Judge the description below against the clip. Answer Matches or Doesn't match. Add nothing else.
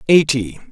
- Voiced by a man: Matches